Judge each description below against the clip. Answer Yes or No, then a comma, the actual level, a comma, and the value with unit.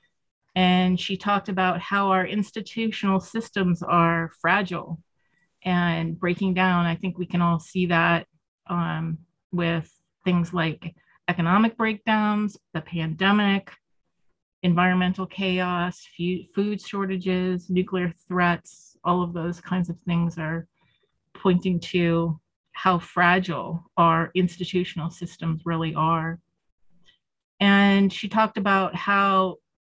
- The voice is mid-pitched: Yes, medium, 180 Hz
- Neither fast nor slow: No, slow, 110 wpm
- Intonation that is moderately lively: No, narrow, 2.2 semitones